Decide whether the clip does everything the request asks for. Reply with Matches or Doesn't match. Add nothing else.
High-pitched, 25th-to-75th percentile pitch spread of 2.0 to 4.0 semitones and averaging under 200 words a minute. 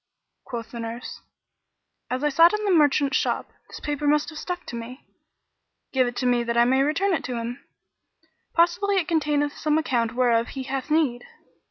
Doesn't match